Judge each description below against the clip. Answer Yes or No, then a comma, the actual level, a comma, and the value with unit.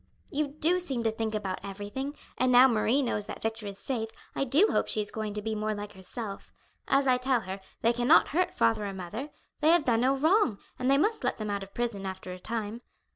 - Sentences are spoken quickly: Yes, fast, 235 wpm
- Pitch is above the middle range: Yes, high, 225 Hz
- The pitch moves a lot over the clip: No, average, 4.8 semitones